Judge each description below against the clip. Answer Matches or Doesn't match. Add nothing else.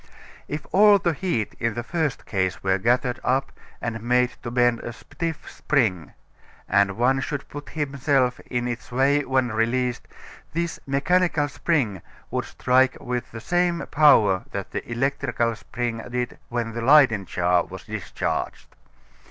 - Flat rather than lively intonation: Doesn't match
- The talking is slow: Doesn't match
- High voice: Doesn't match